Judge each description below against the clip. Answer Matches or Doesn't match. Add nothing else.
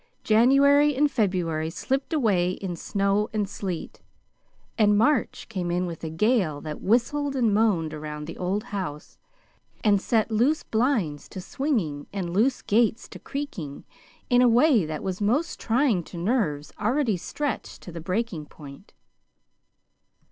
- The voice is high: Matches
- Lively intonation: Matches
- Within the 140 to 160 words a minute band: Matches